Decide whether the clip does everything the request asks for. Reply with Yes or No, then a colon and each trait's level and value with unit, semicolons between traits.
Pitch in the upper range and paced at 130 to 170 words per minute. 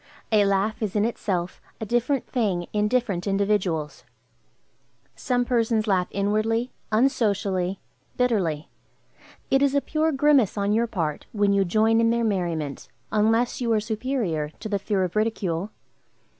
Yes: high, 215 Hz; average, 145 wpm